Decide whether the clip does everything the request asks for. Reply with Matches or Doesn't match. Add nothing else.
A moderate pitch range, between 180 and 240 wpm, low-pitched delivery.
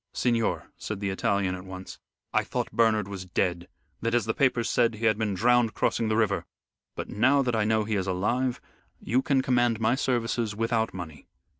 Matches